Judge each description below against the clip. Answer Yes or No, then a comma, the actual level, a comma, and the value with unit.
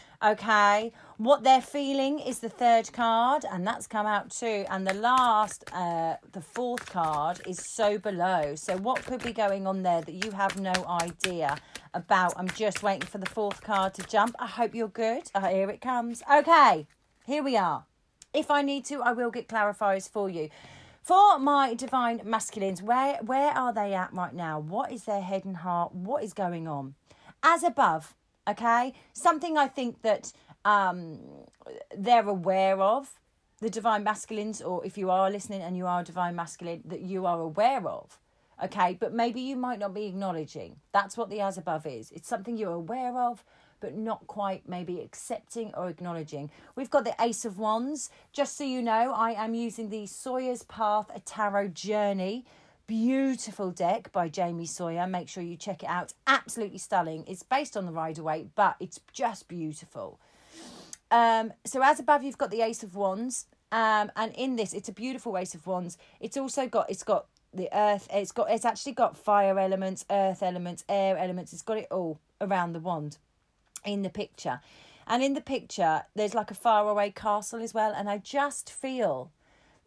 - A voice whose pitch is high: Yes, high, 210 Hz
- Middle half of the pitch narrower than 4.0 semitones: No, average, 4.4 semitones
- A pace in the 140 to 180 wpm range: No, average, 190 wpm